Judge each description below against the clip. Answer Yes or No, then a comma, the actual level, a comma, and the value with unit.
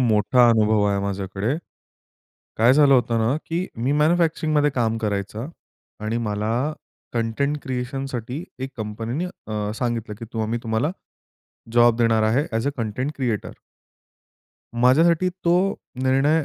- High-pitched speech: No, low, 120 Hz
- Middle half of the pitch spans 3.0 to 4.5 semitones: Yes, average, 4.2 semitones